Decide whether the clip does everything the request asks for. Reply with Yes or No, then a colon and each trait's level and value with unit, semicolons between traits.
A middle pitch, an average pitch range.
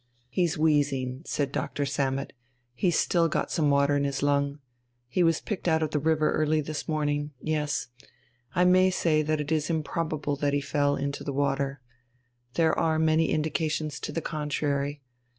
No: medium, 150 Hz; narrow, 1.9 semitones